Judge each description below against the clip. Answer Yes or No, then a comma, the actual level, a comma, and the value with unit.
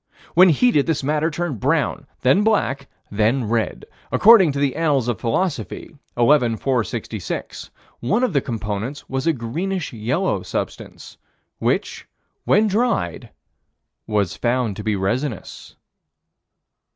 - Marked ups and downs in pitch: Yes, wide, 6.3 semitones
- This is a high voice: No, low, 135 Hz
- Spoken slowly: Yes, slow, 125 wpm